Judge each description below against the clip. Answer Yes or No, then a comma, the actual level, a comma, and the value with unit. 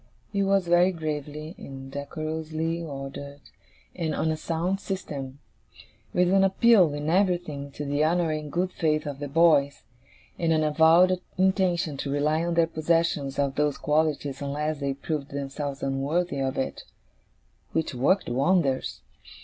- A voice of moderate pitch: Yes, medium, 155 Hz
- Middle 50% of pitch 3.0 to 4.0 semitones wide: Yes, average, 3.3 semitones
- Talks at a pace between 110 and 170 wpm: Yes, average, 150 wpm